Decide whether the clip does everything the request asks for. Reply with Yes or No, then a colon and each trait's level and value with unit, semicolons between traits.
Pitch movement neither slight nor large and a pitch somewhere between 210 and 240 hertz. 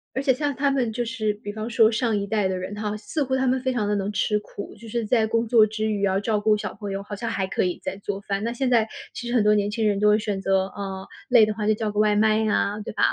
No: narrow, 2.2 semitones; high, 215 Hz